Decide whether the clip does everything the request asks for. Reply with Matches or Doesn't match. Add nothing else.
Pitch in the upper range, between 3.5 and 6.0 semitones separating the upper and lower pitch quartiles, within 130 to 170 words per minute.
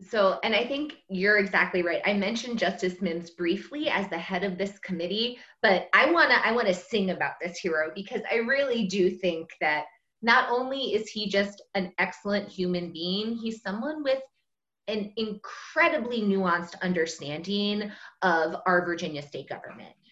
Matches